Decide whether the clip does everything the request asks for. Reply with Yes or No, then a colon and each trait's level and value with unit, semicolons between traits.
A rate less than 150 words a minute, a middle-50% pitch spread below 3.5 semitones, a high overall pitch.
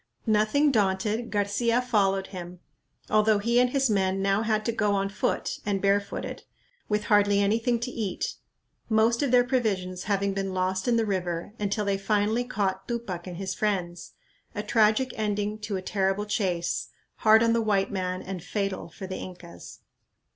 No: average, 170 wpm; narrow, 2.4 semitones; high, 205 Hz